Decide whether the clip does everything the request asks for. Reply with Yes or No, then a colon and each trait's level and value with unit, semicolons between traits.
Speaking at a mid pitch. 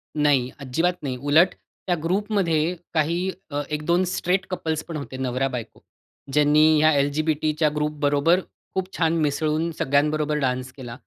Yes: medium, 150 Hz